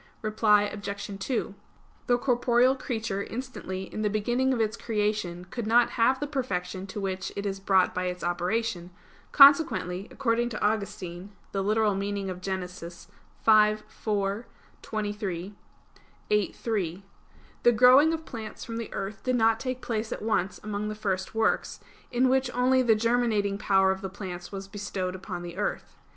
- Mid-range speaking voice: No, high, 210 Hz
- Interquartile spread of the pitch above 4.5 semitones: No, average, 3.3 semitones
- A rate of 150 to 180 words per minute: Yes, average, 160 wpm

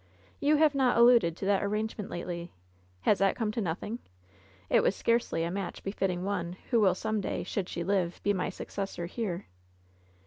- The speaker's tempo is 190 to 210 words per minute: Yes, average, 195 wpm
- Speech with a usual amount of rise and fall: Yes, average, 3.8 semitones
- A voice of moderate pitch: No, high, 200 Hz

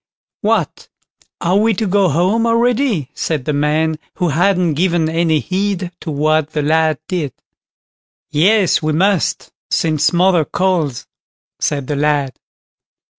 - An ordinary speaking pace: No, slow, 130 wpm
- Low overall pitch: No, medium, 165 Hz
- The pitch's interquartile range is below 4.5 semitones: Yes, average, 3.9 semitones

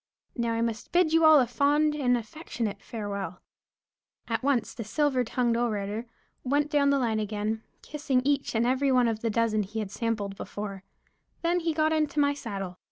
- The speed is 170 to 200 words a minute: Yes, average, 185 wpm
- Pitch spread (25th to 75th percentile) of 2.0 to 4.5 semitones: No, average, 4.9 semitones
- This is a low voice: No, high, 235 Hz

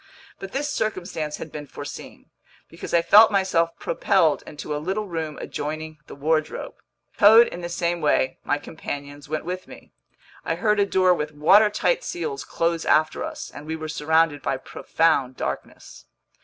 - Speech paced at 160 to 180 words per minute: Yes, average, 165 wpm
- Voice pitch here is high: No, medium, 165 Hz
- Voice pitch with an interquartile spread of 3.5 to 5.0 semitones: Yes, average, 4.1 semitones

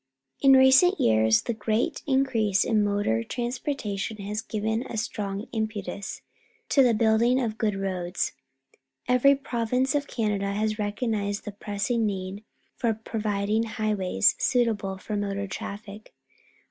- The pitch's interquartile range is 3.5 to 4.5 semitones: No, average, 2.7 semitones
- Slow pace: Yes, slow, 130 wpm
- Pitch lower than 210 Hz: No, high, 215 Hz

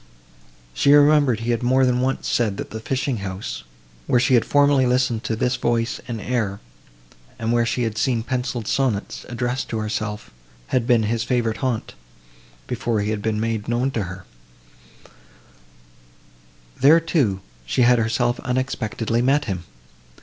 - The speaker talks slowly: No, average, 155 wpm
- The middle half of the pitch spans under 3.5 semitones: Yes, average, 2.7 semitones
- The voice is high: No, low, 120 Hz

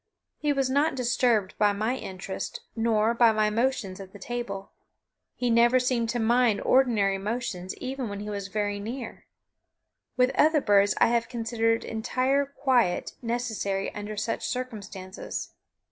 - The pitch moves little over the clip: No, average, 3.6 semitones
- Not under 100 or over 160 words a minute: Yes, average, 145 wpm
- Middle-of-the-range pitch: No, high, 230 Hz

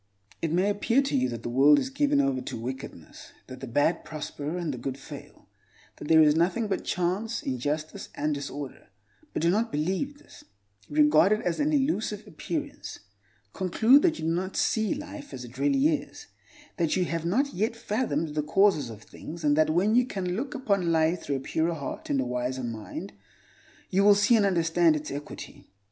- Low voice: No, medium, 170 Hz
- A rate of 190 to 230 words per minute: Yes, average, 195 wpm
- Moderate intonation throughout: No, wide, 6.8 semitones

